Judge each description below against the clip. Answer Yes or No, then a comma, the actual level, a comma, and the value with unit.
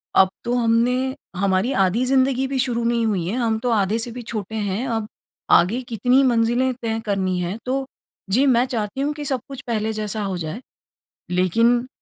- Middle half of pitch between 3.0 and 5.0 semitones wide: Yes, average, 3.4 semitones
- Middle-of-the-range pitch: No, high, 230 Hz